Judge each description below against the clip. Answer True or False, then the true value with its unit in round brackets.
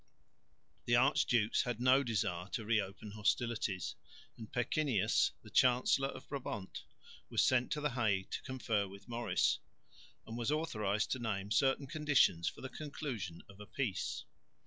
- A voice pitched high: False (115 Hz)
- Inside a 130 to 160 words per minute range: True (150 wpm)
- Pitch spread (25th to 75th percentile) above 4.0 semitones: True (4.4 semitones)